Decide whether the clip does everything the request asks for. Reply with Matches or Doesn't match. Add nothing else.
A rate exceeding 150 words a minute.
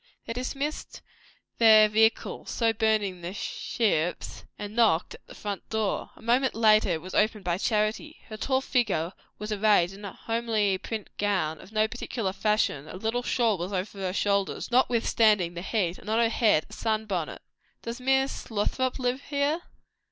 Matches